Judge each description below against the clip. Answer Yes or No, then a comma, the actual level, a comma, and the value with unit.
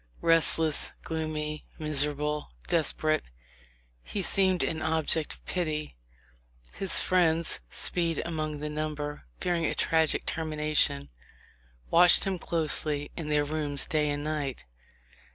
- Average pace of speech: No, slow, 115 wpm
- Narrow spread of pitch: Yes, narrow, 1.7 semitones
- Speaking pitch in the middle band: Yes, medium, 155 Hz